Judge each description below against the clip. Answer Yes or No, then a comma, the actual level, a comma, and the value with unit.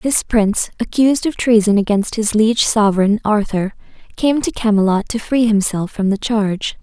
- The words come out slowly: No, average, 165 wpm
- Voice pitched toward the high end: Yes, high, 215 Hz